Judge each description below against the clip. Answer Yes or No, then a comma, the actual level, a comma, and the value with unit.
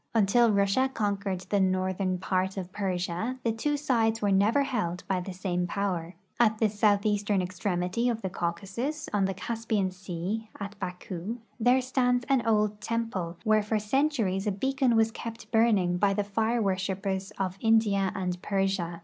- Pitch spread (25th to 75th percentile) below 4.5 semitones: Yes, average, 3.2 semitones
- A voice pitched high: Yes, high, 200 Hz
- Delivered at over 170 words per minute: No, average, 165 wpm